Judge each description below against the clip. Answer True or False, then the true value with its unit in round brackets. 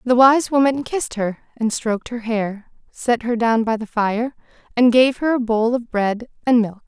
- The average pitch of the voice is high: True (235 Hz)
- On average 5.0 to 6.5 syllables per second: False (4.6 syllables/s)